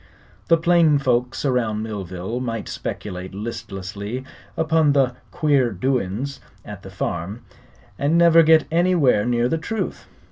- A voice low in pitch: Yes, low, 125 Hz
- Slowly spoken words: Yes, slow, 130 wpm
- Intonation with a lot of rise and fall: Yes, wide, 6.9 semitones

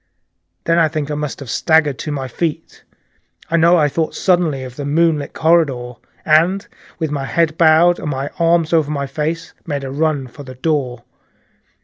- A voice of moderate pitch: Yes, medium, 155 Hz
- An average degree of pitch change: Yes, average, 3.0 semitones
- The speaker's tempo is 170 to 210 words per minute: Yes, average, 190 wpm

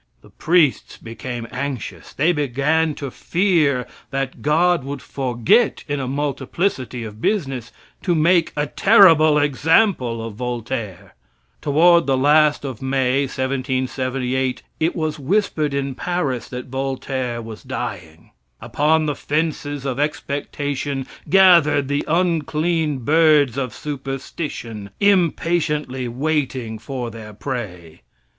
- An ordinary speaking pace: No, slow, 115 wpm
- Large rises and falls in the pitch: No, average, 3.6 semitones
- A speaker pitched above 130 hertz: Yes, medium, 140 Hz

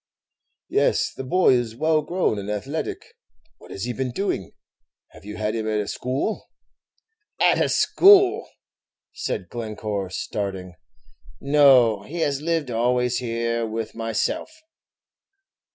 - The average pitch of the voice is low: Yes, low, 120 Hz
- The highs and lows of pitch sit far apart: Yes, wide, 5.7 semitones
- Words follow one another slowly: Yes, slow, 130 wpm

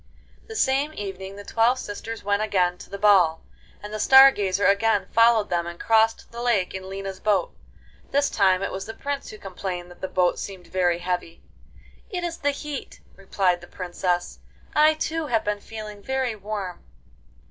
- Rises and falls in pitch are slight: No, average, 3.9 semitones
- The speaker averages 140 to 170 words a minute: No, average, 180 wpm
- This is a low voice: No, high, 205 Hz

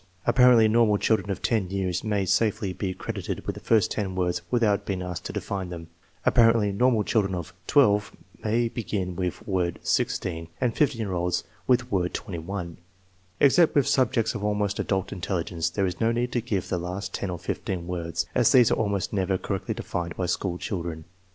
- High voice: No, low, 100 Hz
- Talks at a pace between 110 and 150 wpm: No, average, 200 wpm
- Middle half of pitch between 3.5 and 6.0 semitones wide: Yes, average, 4.0 semitones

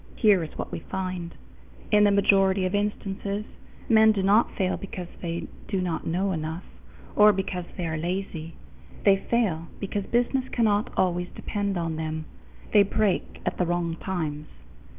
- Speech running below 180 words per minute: Yes, average, 160 wpm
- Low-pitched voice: No, high, 190 Hz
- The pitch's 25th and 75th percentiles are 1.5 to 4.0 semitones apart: Yes, average, 3.2 semitones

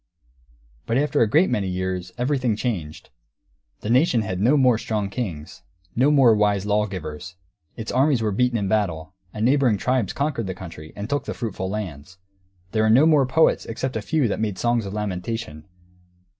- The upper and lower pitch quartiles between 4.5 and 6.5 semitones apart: Yes, average, 5.1 semitones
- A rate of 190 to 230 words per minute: No, average, 180 wpm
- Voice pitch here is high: No, low, 110 Hz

